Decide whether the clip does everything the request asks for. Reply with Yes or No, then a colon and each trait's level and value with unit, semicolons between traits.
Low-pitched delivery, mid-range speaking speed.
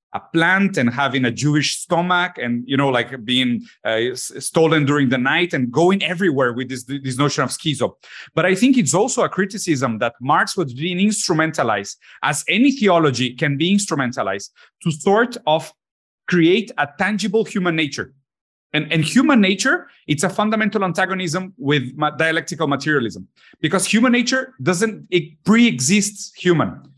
No: medium, 170 Hz; average, 160 wpm